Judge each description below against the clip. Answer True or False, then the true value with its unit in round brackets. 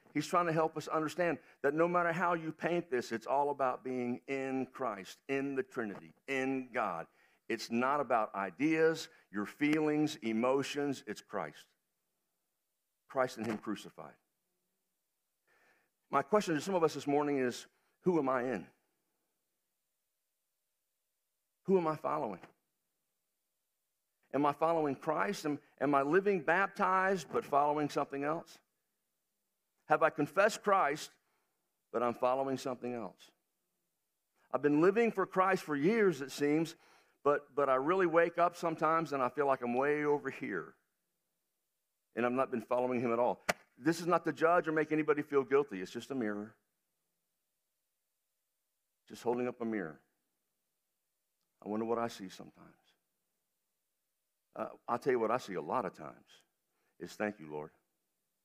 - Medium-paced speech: True (150 wpm)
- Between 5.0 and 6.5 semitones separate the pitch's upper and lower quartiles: True (5.5 semitones)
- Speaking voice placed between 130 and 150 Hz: True (135 Hz)